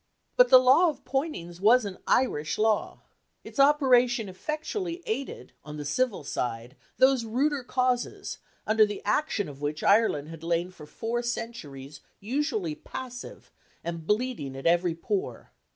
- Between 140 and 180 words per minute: Yes, average, 145 wpm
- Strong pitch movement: Yes, wide, 7.6 semitones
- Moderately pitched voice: No, high, 220 Hz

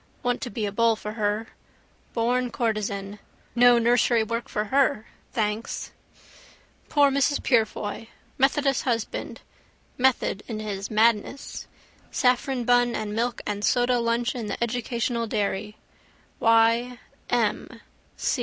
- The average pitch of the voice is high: Yes, high, 230 Hz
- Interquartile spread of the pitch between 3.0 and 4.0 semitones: No, narrow, 2.4 semitones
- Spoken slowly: Yes, slow, 120 wpm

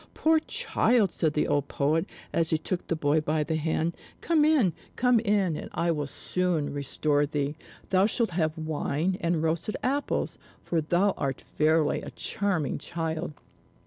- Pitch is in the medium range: Yes, medium, 165 Hz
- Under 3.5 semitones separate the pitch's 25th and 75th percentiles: No, average, 4.4 semitones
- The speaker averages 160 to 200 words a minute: Yes, average, 165 wpm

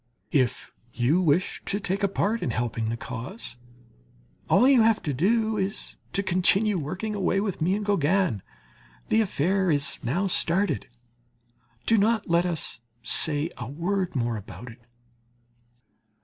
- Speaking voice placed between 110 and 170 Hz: No, medium, 180 Hz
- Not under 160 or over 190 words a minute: No, average, 150 wpm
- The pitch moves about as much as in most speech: No, wide, 6.3 semitones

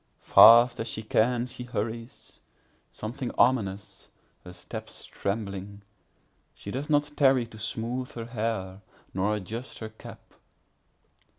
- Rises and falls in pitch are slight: No, average, 3.3 semitones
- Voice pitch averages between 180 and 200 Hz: No, low, 115 Hz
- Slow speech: Yes, slow, 105 wpm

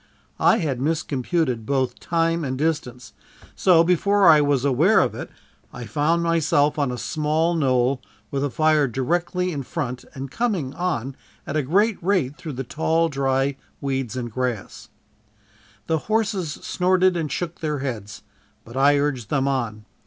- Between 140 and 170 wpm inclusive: Yes, average, 160 wpm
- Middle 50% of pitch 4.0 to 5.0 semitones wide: Yes, average, 4.3 semitones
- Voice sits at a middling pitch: Yes, medium, 145 Hz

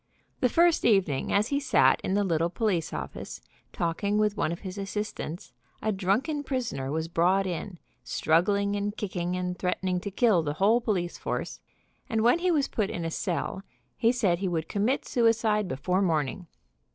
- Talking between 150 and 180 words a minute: Yes, average, 175 wpm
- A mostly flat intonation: No, average, 4.0 semitones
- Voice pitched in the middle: No, high, 195 Hz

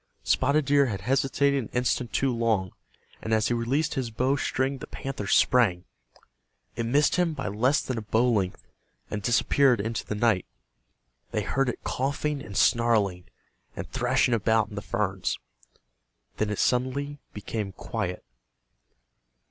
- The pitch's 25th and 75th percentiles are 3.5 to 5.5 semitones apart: Yes, average, 4.3 semitones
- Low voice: Yes, low, 120 Hz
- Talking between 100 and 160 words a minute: Yes, average, 150 wpm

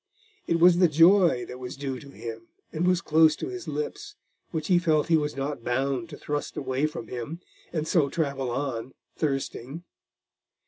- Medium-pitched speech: Yes, medium, 150 Hz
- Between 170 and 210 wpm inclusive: Yes, average, 180 wpm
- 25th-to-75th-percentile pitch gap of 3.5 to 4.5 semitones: Yes, average, 4.1 semitones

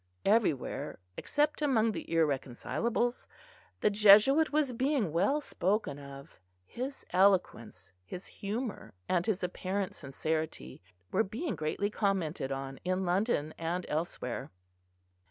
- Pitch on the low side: No, high, 190 Hz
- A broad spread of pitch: Yes, wide, 6.5 semitones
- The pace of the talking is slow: Yes, slow, 115 wpm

